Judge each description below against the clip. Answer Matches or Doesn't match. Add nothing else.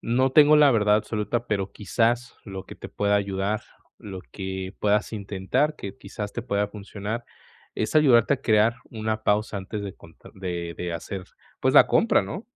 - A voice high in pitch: Doesn't match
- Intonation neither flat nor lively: Matches